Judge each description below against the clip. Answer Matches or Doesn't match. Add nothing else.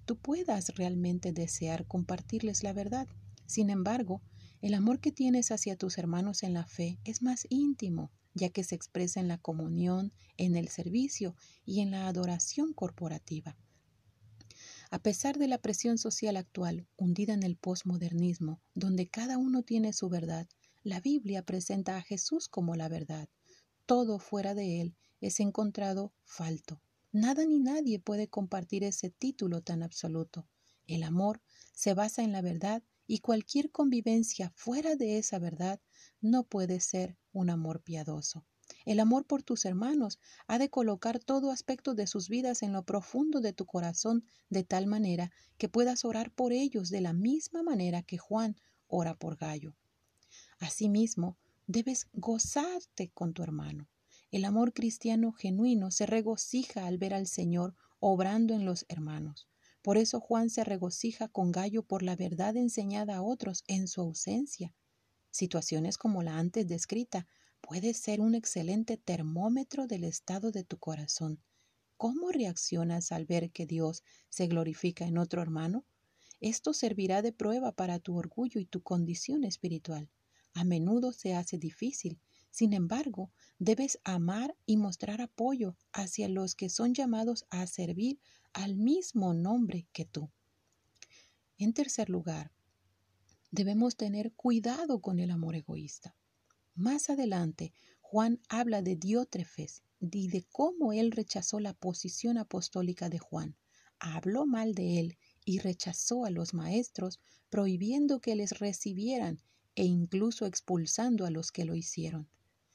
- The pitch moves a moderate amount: Matches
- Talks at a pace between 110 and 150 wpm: Matches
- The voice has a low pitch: Doesn't match